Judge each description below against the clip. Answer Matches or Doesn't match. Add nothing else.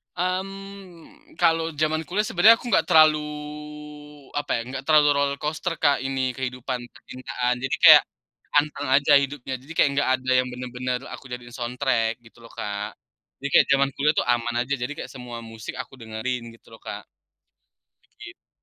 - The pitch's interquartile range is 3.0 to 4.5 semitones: Matches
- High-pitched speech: Doesn't match